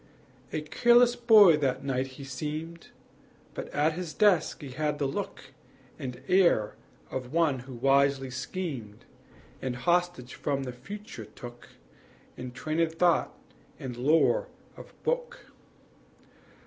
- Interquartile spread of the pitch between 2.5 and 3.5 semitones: No, average, 5.1 semitones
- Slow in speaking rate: Yes, slow, 125 wpm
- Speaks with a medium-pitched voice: Yes, medium, 145 Hz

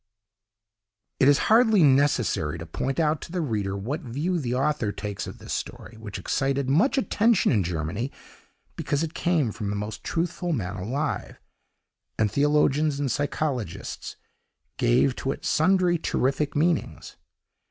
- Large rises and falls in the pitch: Yes, wide, 6.4 semitones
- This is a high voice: No, medium, 140 Hz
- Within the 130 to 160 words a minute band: Yes, average, 145 wpm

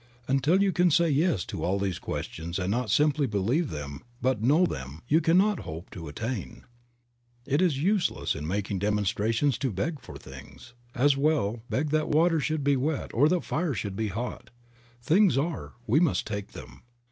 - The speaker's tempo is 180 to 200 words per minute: Yes, average, 190 wpm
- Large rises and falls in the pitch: Yes, wide, 7.6 semitones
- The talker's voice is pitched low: Yes, low, 130 Hz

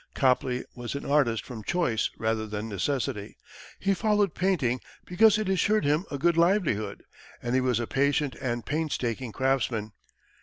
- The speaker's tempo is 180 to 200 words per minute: No, average, 155 wpm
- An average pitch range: No, wide, 6.4 semitones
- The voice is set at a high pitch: No, low, 135 Hz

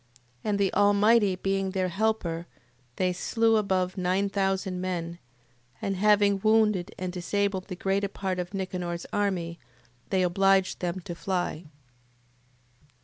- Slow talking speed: Yes, slow, 130 wpm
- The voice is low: No, high, 190 Hz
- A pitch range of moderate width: No, narrow, 2.0 semitones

